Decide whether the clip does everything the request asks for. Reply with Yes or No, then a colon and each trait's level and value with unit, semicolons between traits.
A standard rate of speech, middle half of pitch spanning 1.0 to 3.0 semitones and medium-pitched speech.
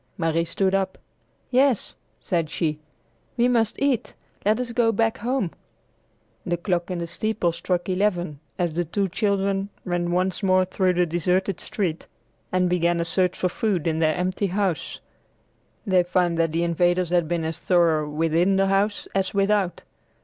Yes: average, 165 wpm; narrow, 2.6 semitones; medium, 180 Hz